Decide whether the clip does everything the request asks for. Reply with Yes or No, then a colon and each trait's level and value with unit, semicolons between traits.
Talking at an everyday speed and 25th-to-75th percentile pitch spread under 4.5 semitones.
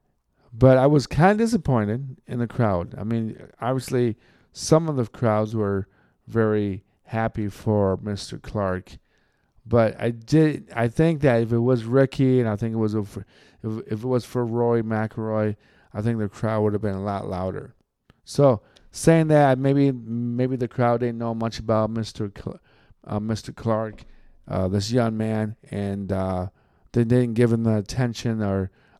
Yes: average, 175 wpm; average, 3.0 semitones